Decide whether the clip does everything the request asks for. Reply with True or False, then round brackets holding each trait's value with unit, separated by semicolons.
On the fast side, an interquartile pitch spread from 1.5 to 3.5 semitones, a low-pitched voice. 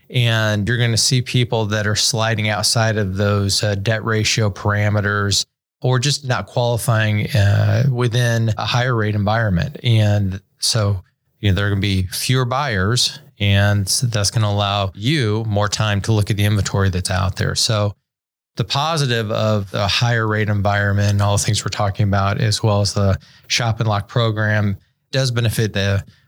False (185 wpm; 2.8 semitones; 105 Hz)